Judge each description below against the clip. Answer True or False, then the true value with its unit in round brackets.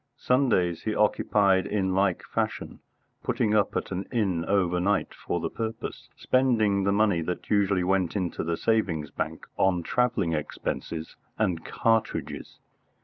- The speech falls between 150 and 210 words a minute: False (140 wpm)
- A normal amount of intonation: True (3.3 semitones)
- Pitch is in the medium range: False (100 Hz)